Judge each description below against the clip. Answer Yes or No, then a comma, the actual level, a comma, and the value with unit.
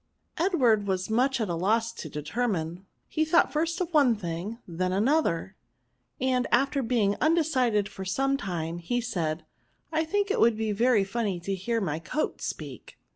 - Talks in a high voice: Yes, high, 225 Hz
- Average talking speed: Yes, average, 180 wpm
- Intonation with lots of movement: Yes, wide, 6.5 semitones